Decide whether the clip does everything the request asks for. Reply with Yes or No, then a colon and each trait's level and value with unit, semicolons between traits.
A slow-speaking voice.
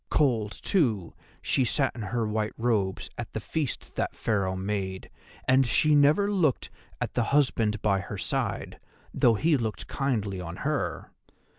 No: average, 155 wpm